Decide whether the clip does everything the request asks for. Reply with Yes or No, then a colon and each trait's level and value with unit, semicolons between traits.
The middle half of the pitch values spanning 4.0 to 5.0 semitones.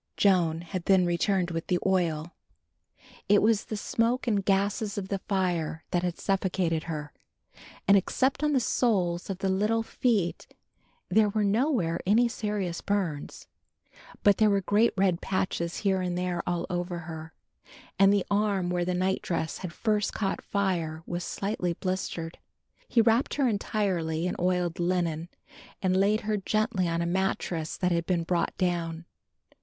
No: average, 3.0 semitones